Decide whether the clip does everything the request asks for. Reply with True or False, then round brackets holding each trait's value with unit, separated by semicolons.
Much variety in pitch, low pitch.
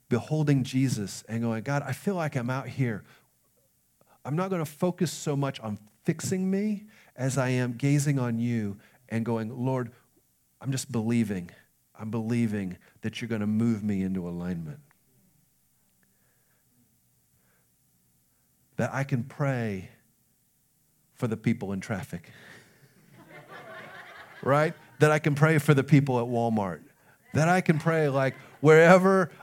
False (5.0 semitones; 125 Hz)